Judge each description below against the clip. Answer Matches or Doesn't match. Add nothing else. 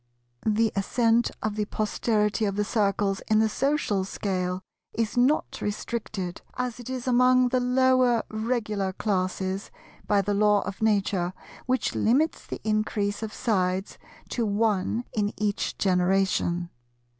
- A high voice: Matches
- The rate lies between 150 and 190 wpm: Doesn't match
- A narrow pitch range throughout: Doesn't match